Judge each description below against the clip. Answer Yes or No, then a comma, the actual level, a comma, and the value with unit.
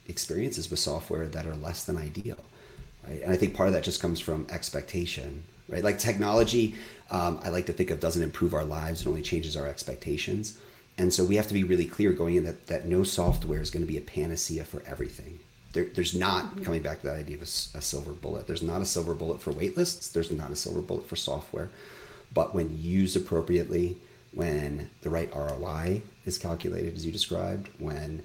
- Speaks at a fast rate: Yes, fast, 215 wpm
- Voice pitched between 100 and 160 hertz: No, very low, 85 Hz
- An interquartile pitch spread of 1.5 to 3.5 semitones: Yes, average, 2.8 semitones